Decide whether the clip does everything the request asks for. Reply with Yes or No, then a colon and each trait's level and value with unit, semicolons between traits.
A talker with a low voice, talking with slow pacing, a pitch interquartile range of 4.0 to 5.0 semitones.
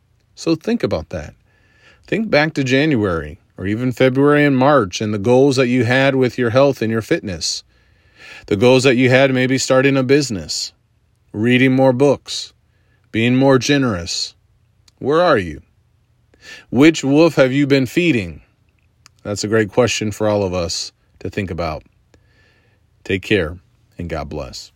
No: low, 115 Hz; average, 160 wpm; average, 4.3 semitones